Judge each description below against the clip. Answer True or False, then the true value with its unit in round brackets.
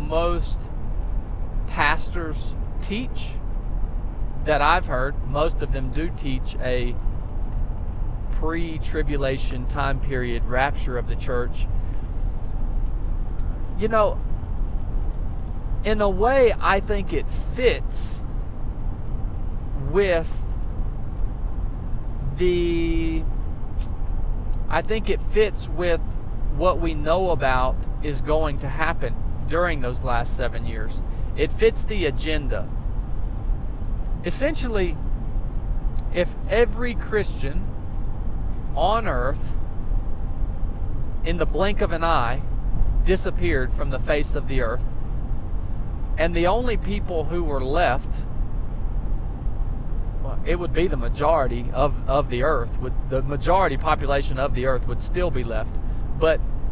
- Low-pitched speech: True (120 Hz)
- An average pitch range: False (6.8 semitones)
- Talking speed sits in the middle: False (105 wpm)